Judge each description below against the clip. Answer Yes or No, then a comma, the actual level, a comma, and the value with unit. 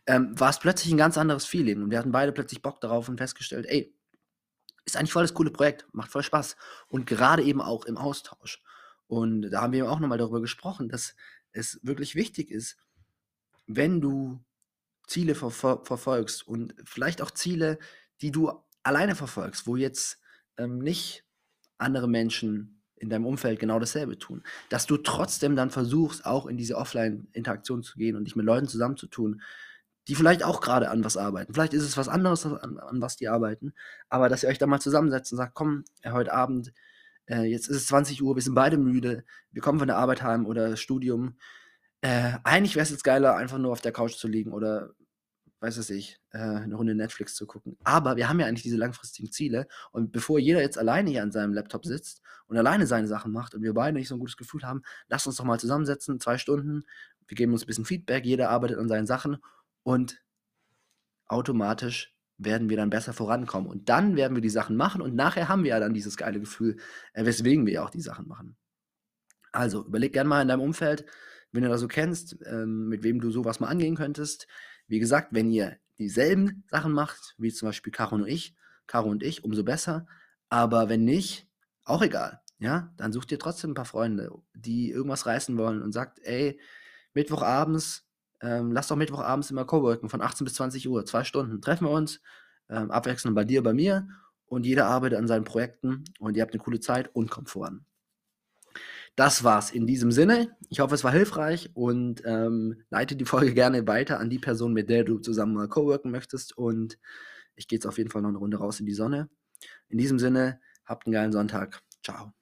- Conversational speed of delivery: No, fast, 205 wpm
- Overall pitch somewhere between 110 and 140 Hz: Yes, low, 125 Hz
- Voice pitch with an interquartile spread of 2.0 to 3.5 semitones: No, average, 4.2 semitones